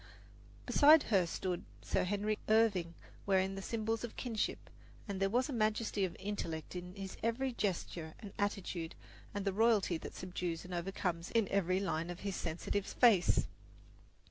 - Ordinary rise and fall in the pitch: Yes, average, 3.3 semitones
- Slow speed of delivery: No, average, 155 wpm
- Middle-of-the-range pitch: No, high, 195 Hz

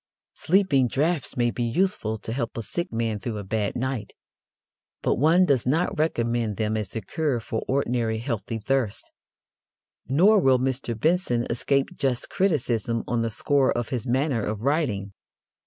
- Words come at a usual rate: Yes, average, 160 wpm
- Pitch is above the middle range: No, low, 120 Hz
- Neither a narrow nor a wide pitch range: Yes, average, 4.1 semitones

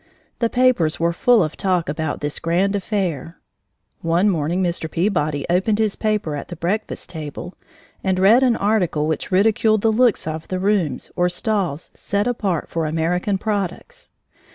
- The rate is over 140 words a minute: Yes, average, 160 wpm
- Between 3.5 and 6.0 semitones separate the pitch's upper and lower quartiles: Yes, average, 4.4 semitones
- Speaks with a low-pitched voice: No, medium, 185 Hz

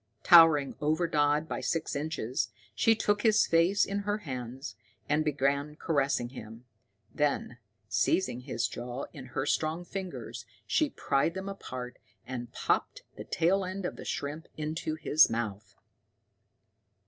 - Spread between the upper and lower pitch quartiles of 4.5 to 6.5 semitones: Yes, average, 5.2 semitones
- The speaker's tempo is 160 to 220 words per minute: No, average, 140 wpm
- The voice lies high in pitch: No, medium, 150 Hz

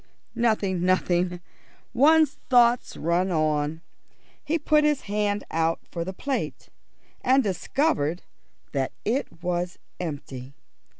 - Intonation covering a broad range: Yes, wide, 7.0 semitones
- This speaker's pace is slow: Yes, slow, 110 wpm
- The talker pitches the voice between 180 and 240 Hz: Yes, medium, 185 Hz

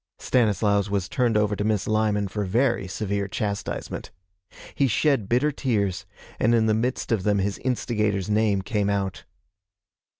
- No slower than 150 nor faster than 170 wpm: Yes, average, 155 wpm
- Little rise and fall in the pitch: Yes, narrow, 2.3 semitones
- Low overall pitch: Yes, low, 105 Hz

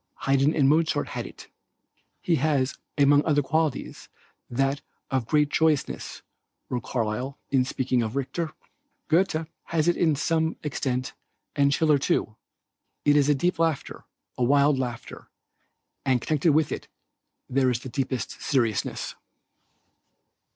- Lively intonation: No, average, 3.2 semitones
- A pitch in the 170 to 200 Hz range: No, medium, 140 Hz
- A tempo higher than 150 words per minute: No, slow, 135 wpm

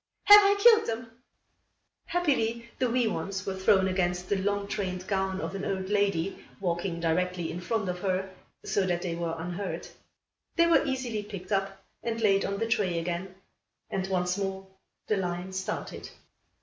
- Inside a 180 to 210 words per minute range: No, average, 170 wpm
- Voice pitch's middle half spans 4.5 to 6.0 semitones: No, average, 2.8 semitones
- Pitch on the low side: No, high, 195 Hz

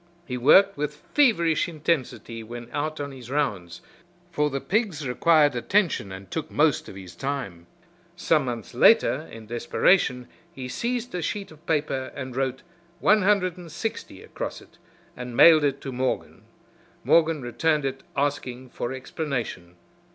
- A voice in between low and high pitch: Yes, medium, 145 Hz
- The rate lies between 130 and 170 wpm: Yes, average, 145 wpm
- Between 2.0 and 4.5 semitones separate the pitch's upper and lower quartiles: No, average, 4.9 semitones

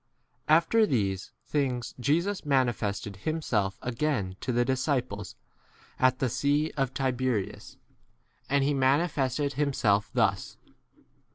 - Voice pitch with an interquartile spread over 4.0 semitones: No, average, 3.6 semitones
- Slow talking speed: Yes, slow, 105 wpm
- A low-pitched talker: Yes, low, 130 Hz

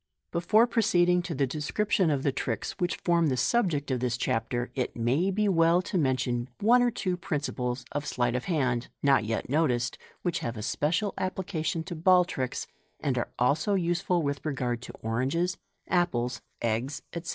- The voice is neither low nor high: Yes, medium, 150 Hz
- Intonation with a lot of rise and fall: Yes, wide, 6.1 semitones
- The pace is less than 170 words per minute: No, average, 175 wpm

